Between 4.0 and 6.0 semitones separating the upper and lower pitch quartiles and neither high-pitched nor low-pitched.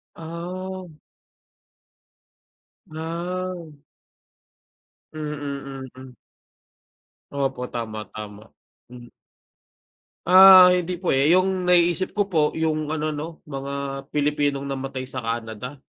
Yes: average, 4.7 semitones; medium, 150 Hz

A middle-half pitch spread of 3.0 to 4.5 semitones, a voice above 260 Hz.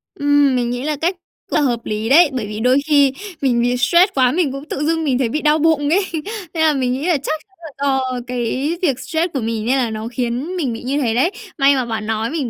Yes: average, 4.0 semitones; very high, 270 Hz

